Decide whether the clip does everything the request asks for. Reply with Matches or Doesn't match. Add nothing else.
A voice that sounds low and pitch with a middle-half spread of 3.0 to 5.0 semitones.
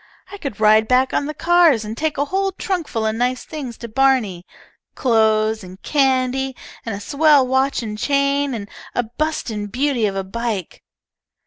Doesn't match